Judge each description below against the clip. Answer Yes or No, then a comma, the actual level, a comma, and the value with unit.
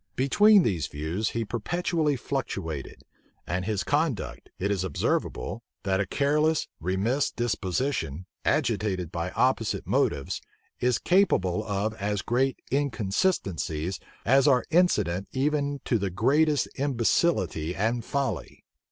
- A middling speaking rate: No, slow, 120 wpm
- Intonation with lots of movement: Yes, wide, 6.9 semitones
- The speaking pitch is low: Yes, low, 115 Hz